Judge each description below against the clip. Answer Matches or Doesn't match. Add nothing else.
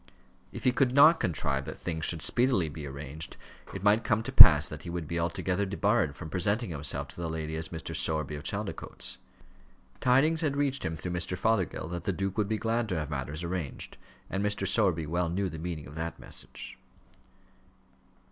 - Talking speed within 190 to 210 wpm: Matches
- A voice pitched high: Doesn't match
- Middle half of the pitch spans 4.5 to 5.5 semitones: Matches